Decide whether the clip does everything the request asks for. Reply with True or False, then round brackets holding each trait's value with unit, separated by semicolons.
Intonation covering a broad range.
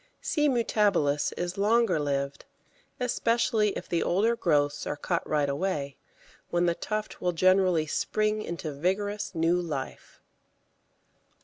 True (5.8 semitones)